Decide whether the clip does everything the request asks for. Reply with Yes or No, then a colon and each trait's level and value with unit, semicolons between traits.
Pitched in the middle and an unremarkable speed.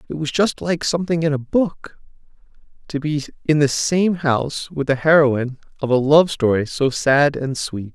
Yes: medium, 145 Hz; average, 190 wpm